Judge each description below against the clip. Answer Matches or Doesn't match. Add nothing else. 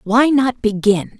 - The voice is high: Matches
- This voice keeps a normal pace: Matches